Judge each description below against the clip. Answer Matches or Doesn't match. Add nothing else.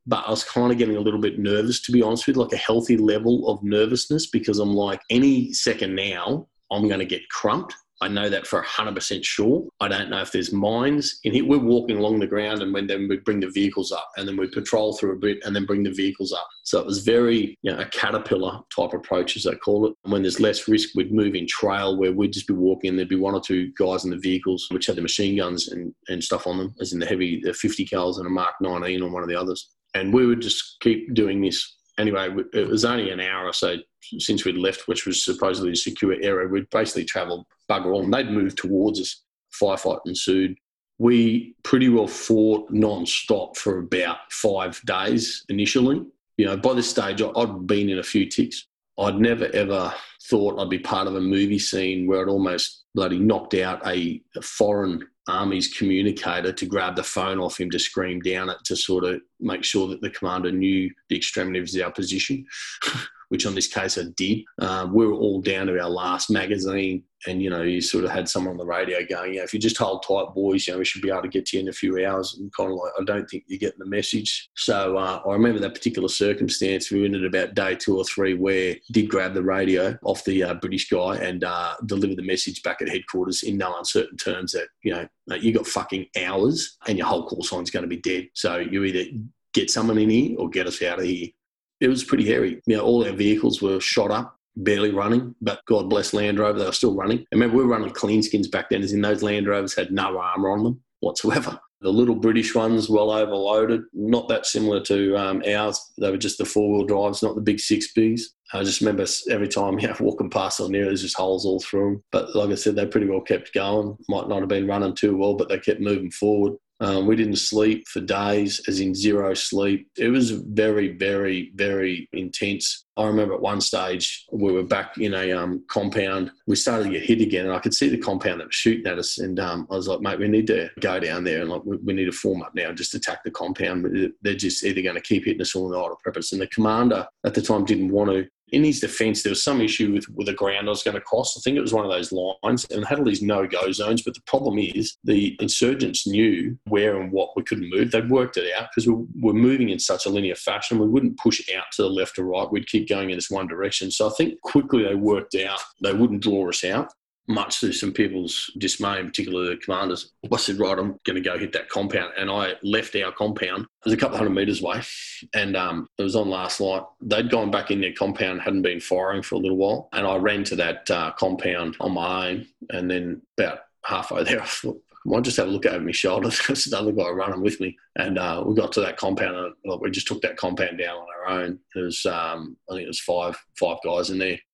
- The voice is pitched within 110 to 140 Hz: Doesn't match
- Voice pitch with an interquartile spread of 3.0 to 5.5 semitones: Doesn't match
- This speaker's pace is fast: Matches